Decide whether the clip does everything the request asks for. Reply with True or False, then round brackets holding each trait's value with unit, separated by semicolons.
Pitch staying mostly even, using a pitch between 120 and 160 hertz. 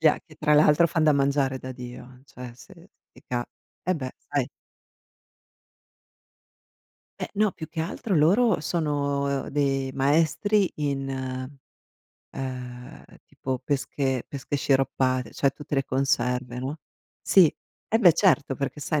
False (3.2 semitones; 140 Hz)